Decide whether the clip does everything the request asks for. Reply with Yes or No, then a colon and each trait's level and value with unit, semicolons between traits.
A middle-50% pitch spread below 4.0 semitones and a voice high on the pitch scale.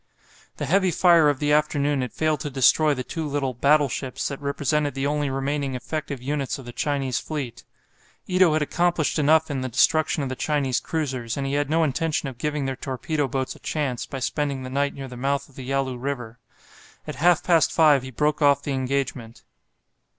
No: narrow, 2.4 semitones; medium, 140 Hz